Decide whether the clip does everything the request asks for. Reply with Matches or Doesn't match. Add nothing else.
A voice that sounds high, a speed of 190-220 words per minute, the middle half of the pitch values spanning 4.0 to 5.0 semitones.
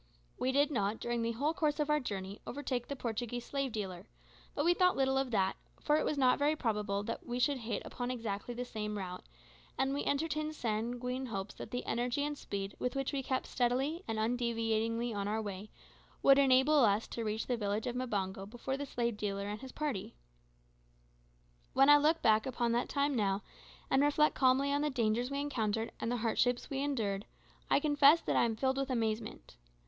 Matches